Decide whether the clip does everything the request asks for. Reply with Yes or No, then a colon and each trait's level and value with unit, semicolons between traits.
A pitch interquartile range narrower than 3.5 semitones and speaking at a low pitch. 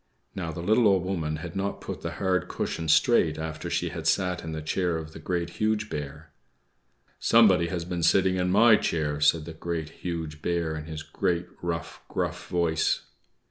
Yes: narrow, 2.6 semitones; very low, 85 Hz